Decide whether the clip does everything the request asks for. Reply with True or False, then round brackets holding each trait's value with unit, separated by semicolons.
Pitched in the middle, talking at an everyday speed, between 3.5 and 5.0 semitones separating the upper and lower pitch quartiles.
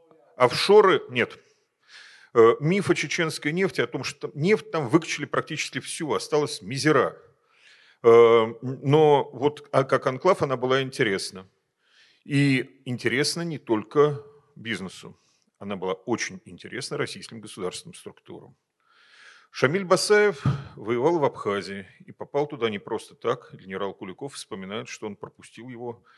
True (145 Hz; 120 wpm; 4.7 semitones)